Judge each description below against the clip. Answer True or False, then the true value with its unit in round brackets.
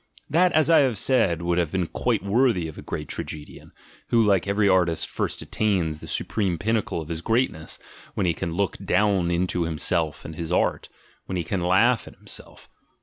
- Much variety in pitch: False (4.3 semitones)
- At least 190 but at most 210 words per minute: True (195 wpm)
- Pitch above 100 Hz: False (95 Hz)